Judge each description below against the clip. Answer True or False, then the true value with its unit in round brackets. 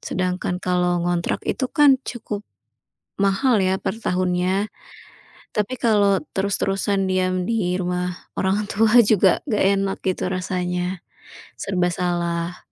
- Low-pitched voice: False (185 Hz)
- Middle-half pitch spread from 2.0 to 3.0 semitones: True (2.4 semitones)